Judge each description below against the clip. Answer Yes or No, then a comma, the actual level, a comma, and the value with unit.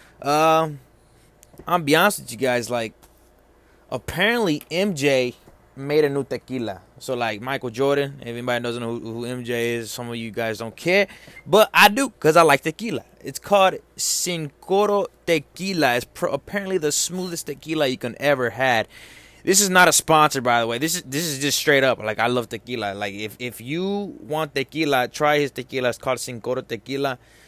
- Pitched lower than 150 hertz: Yes, medium, 140 Hz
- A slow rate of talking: No, average, 190 wpm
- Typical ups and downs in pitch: Yes, average, 4.9 semitones